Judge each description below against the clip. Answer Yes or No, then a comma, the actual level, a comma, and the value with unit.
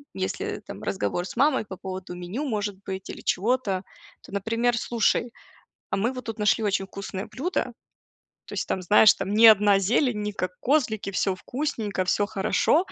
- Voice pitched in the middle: No, high, 210 Hz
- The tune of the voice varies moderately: Yes, average, 3.9 semitones